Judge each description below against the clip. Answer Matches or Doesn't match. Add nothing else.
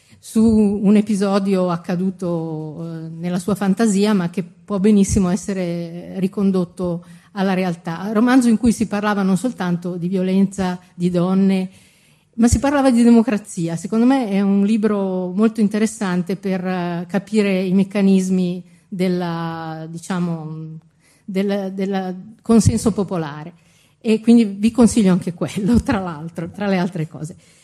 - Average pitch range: Matches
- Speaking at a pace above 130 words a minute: Doesn't match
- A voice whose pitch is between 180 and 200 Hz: Matches